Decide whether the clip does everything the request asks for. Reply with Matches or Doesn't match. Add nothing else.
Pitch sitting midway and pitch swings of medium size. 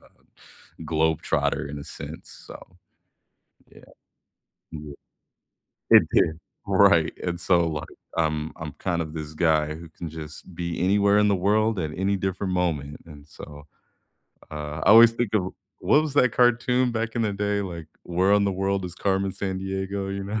Doesn't match